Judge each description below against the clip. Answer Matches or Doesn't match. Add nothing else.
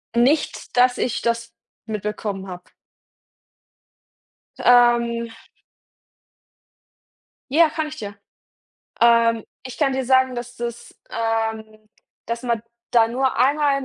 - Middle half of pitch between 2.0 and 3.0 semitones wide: Matches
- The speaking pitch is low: Doesn't match